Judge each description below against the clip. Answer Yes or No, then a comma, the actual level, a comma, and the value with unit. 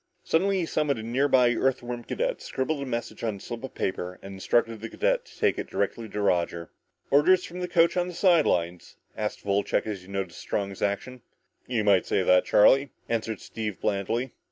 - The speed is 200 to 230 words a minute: Yes, fast, 205 wpm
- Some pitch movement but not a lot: No, wide, 6.2 semitones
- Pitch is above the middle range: No, low, 115 Hz